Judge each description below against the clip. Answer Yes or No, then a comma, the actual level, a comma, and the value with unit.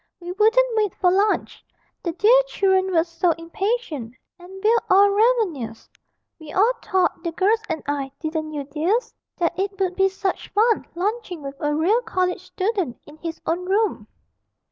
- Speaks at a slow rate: No, average, 165 wpm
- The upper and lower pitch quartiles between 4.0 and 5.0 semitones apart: Yes, average, 4.3 semitones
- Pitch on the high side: Yes, very high, 370 Hz